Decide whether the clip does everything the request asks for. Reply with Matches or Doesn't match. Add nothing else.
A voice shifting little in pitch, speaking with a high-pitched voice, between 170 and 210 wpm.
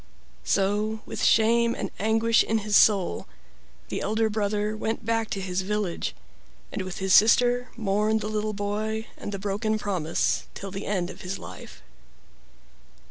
Doesn't match